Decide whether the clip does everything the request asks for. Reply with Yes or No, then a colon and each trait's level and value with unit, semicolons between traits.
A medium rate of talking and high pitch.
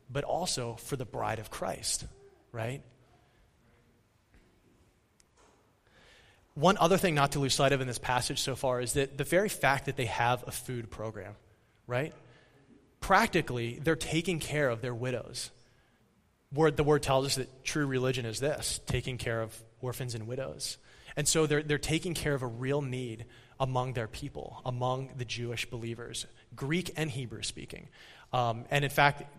No: average, 165 wpm; low, 130 Hz